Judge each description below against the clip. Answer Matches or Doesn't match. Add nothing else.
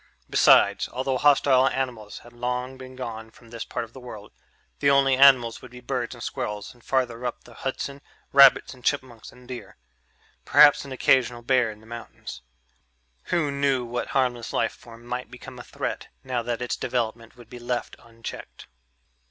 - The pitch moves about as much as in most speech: Doesn't match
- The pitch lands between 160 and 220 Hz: Doesn't match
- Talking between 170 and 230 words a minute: Matches